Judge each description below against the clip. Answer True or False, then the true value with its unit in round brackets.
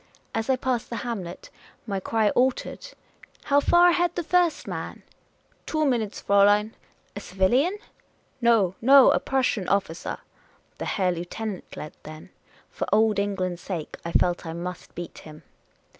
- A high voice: True (210 Hz)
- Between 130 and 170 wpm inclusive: True (165 wpm)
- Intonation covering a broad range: True (6.2 semitones)